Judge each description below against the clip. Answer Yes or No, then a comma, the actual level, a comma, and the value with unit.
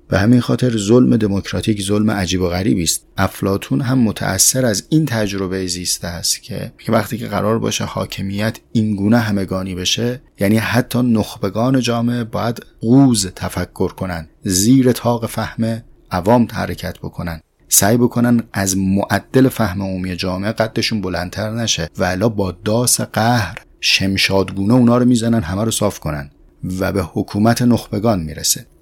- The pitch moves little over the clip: No, average, 3.9 semitones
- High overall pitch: No, low, 105 Hz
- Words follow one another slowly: No, average, 145 wpm